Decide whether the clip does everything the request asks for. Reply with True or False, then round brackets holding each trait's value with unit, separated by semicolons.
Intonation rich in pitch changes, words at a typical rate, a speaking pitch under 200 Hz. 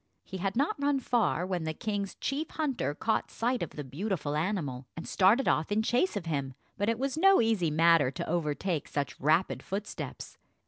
True (6.8 semitones; 190 wpm; 190 Hz)